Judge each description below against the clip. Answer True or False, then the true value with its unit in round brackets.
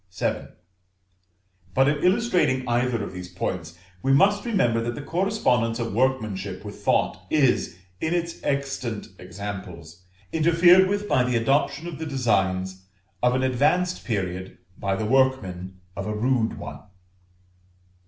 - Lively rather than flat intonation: True (7.3 semitones)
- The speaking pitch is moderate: False (125 Hz)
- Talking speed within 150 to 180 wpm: False (135 wpm)